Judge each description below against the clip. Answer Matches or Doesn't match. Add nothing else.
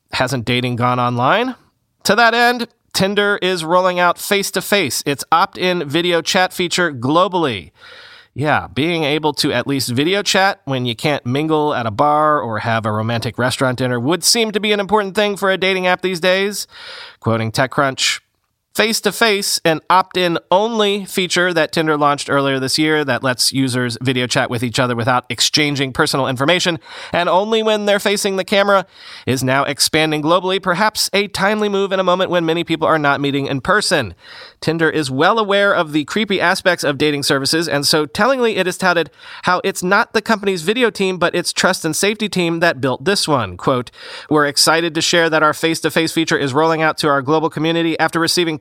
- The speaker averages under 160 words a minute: Doesn't match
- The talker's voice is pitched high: Doesn't match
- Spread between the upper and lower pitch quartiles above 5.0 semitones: Matches